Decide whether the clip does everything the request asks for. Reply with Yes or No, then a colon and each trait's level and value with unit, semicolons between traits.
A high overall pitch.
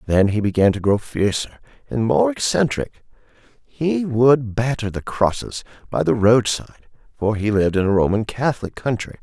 No: low, 110 Hz